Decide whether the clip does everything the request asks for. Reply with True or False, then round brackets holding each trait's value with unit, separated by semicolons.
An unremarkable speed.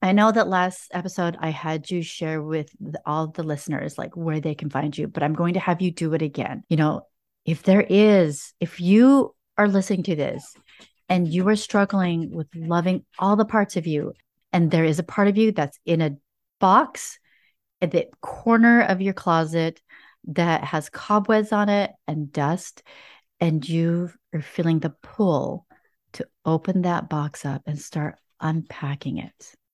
True (180 wpm)